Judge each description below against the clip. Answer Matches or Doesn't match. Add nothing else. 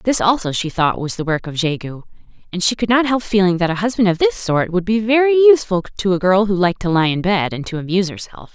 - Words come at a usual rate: Doesn't match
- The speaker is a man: Doesn't match